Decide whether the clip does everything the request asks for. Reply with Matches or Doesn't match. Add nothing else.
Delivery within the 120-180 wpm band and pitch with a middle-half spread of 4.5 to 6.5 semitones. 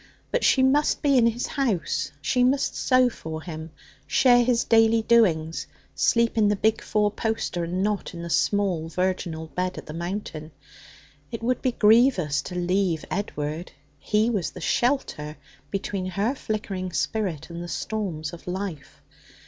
Matches